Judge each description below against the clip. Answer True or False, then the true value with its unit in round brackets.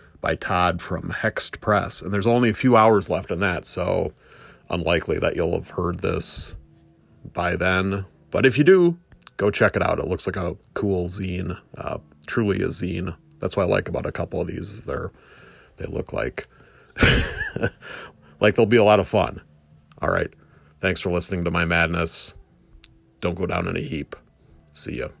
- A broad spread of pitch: False (3.3 semitones)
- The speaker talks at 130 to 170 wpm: False (185 wpm)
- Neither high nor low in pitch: False (95 Hz)